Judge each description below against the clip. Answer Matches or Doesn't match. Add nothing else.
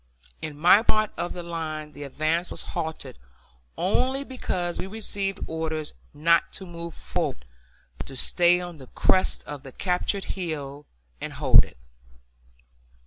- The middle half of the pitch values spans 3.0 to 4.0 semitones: Matches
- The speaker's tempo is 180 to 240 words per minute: Doesn't match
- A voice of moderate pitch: Matches